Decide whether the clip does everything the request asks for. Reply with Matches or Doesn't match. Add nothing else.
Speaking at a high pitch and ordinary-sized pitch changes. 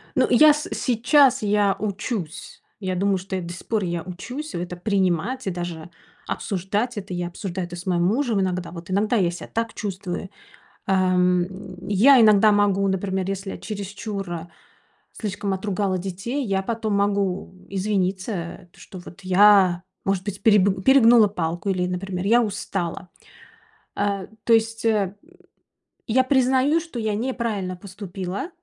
Matches